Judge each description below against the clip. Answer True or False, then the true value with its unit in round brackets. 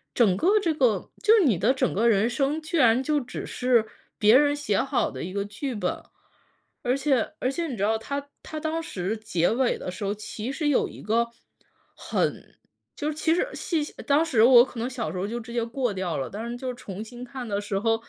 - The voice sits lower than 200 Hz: False (240 Hz)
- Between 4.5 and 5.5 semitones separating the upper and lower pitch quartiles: True (4.8 semitones)